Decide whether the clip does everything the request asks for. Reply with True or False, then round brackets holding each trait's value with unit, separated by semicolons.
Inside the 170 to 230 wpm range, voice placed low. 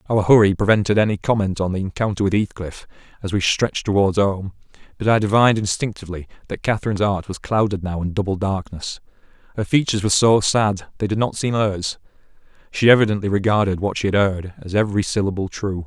True (185 wpm; 100 Hz)